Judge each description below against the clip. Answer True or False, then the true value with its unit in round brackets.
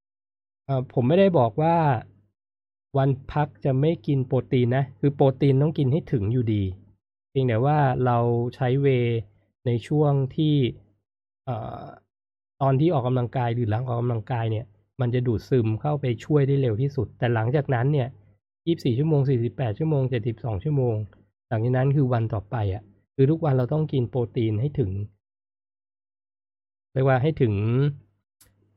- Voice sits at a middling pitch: False (125 Hz)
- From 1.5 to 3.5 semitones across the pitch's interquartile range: False (4.7 semitones)